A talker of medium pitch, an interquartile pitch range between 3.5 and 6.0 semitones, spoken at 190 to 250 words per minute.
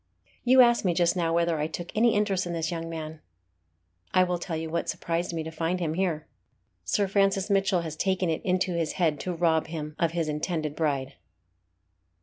No: medium, 170 Hz; narrow, 2.4 semitones; average, 200 wpm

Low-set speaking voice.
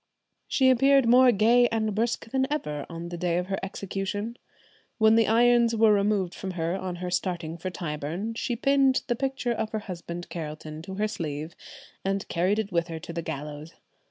No: high, 195 Hz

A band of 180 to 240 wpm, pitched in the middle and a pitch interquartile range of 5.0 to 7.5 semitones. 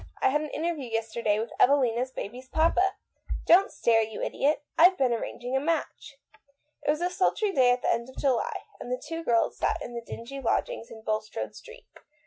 No: average, 200 wpm; very high, 260 Hz; average, 5.3 semitones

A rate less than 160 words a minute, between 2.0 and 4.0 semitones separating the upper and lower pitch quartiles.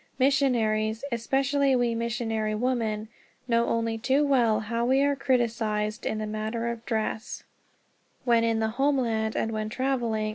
Yes: average, 145 wpm; average, 2.7 semitones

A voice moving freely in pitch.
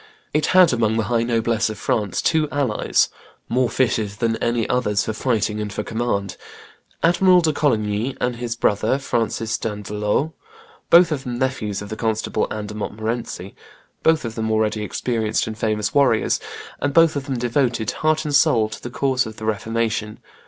No: average, 3.5 semitones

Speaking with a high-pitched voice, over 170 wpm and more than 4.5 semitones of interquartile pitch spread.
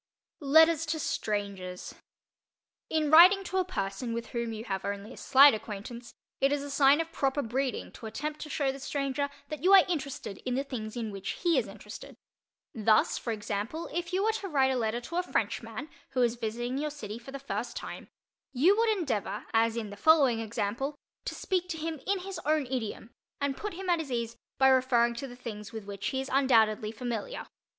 Yes: very high, 265 Hz; fast, 205 wpm; wide, 5.4 semitones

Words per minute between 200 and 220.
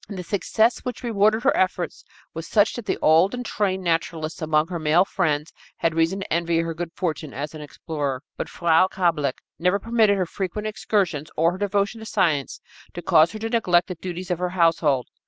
Yes: fast, 205 wpm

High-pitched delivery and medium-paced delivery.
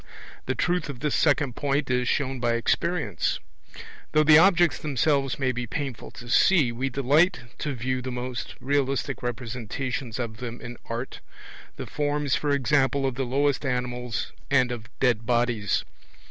No: low, 130 Hz; average, 160 wpm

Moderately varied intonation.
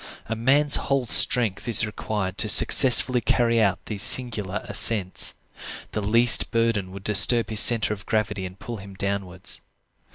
Yes: average, 3.1 semitones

